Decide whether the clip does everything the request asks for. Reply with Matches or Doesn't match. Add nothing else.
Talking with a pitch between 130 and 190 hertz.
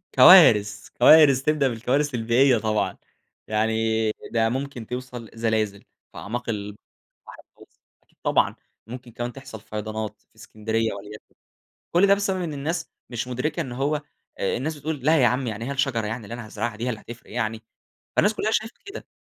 Doesn't match